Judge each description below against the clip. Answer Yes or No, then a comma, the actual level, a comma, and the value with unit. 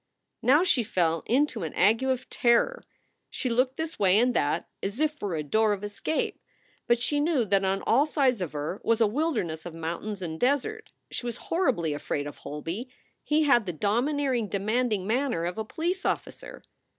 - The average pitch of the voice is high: Yes, high, 225 Hz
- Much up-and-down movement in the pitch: Yes, wide, 6.7 semitones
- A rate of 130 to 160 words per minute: No, average, 185 wpm